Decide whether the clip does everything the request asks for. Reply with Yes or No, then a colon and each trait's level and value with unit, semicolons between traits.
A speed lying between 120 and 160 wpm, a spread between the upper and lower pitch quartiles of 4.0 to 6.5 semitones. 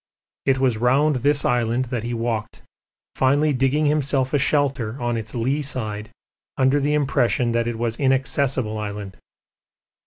No: average, 150 wpm; average, 3.2 semitones